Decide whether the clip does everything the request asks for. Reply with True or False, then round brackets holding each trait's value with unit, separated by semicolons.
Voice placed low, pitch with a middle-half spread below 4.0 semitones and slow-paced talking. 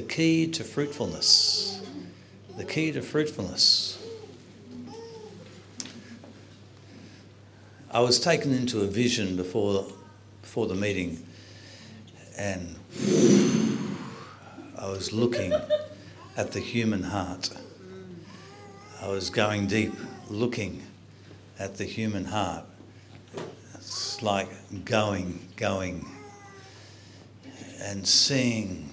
True (105 Hz; 3.4 semitones; 85 wpm)